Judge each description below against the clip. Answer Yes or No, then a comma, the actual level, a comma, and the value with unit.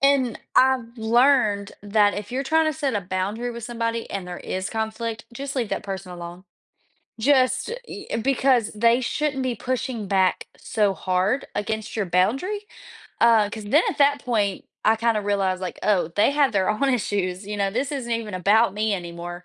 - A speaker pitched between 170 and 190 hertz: No, high, 220 Hz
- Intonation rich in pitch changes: No, average, 4.4 semitones